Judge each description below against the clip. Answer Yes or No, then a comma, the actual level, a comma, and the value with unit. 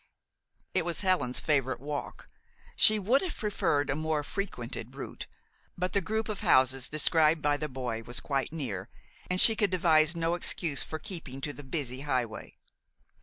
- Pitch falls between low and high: Yes, medium, 150 Hz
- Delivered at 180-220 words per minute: No, average, 170 wpm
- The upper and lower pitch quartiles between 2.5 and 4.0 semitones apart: No, average, 5.2 semitones